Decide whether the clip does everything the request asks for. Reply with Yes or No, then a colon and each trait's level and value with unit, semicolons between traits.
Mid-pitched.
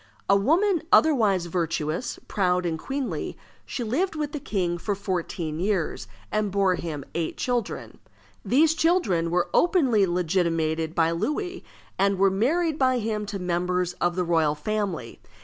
No: high, 195 Hz